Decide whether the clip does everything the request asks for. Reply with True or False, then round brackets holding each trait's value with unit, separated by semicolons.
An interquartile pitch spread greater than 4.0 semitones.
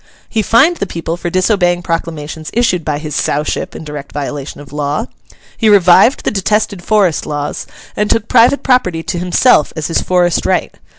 True (5.5 semitones)